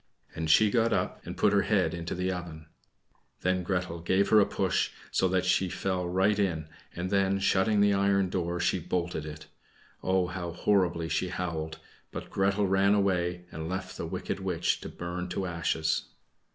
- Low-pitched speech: Yes, very low, 90 Hz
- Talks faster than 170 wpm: Yes, average, 180 wpm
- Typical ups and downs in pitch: No, narrow, 2.2 semitones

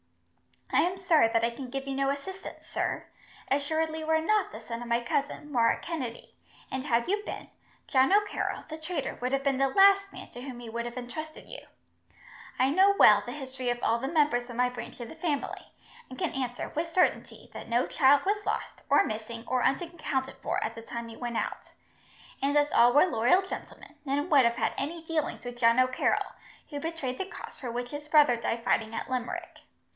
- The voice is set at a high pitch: Yes, very high, 270 Hz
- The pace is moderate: No, fast, 210 wpm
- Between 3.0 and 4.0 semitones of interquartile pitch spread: No, average, 4.7 semitones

